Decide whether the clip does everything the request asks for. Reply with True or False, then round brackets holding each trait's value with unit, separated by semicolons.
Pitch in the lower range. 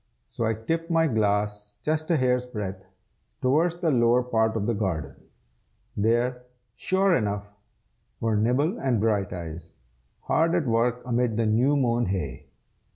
True (115 Hz)